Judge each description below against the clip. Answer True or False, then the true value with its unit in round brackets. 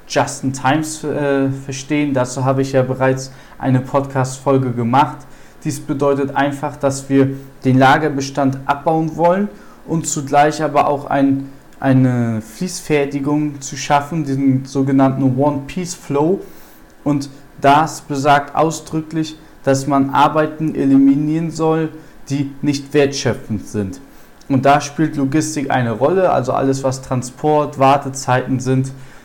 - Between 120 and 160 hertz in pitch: True (140 Hz)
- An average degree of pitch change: False (1.9 semitones)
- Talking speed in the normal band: False (120 wpm)